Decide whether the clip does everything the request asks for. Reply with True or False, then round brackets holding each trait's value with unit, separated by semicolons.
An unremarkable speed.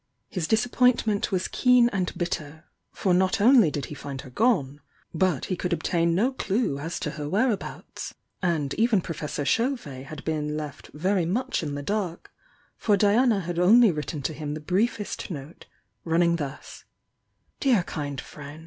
True (160 wpm)